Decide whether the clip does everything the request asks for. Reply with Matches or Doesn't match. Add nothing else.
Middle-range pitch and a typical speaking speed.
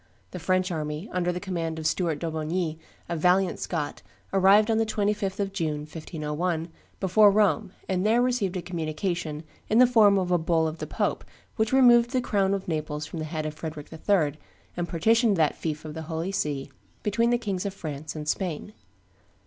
Matches